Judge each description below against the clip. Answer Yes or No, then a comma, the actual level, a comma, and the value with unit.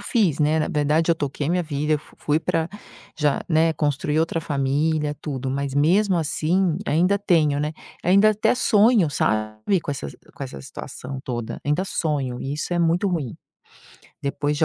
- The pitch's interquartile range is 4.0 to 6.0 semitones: No, average, 3.2 semitones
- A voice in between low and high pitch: Yes, medium, 155 Hz